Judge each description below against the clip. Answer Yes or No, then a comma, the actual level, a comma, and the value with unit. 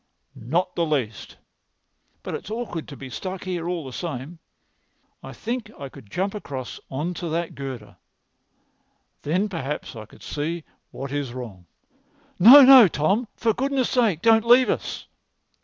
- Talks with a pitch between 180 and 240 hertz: No, medium, 170 Hz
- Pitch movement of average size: No, wide, 7.6 semitones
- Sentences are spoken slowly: No, average, 155 wpm